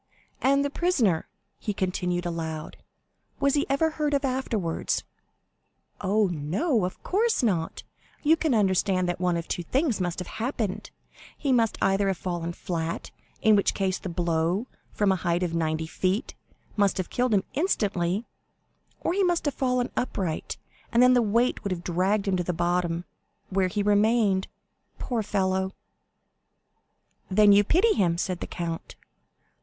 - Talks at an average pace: Yes, average, 160 wpm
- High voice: Yes, high, 195 Hz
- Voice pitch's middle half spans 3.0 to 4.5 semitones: No, wide, 5.6 semitones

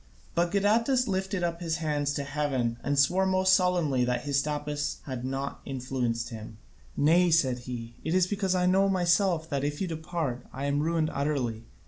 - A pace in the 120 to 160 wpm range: No, average, 175 wpm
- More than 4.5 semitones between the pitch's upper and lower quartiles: Yes, average, 5.2 semitones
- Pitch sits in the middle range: Yes, medium, 150 Hz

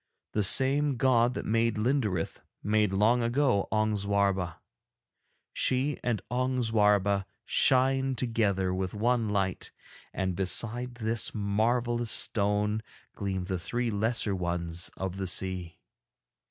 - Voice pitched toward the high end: No, low, 105 Hz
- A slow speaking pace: Yes, slow, 120 wpm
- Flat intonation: No, average, 3.8 semitones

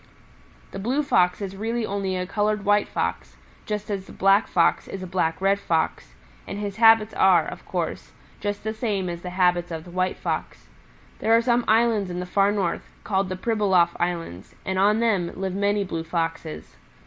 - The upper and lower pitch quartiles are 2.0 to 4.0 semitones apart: Yes, average, 2.9 semitones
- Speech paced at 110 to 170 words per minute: No, average, 195 wpm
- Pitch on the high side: Yes, high, 195 Hz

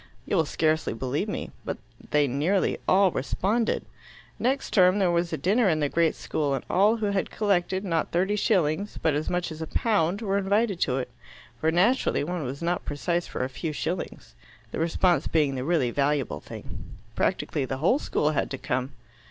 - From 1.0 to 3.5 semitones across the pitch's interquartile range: No, average, 5.1 semitones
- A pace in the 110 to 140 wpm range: No, average, 195 wpm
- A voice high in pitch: No, medium, 170 Hz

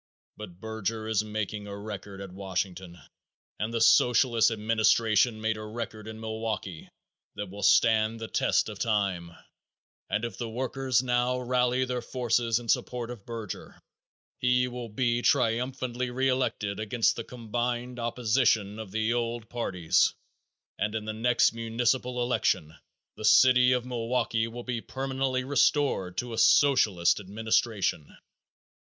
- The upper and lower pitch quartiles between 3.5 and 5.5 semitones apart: No, narrow, 2.5 semitones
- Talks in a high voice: No, low, 115 Hz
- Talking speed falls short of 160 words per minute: Yes, average, 140 wpm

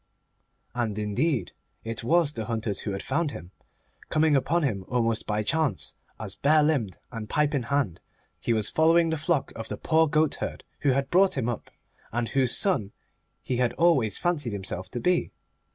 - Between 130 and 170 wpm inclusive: No, average, 180 wpm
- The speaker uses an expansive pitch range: Yes, wide, 6.1 semitones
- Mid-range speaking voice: No, low, 130 Hz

